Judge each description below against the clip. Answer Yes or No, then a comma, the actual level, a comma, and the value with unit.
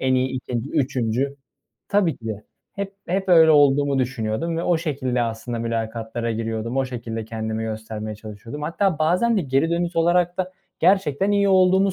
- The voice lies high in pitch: No, low, 135 Hz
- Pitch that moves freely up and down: Yes, wide, 7.2 semitones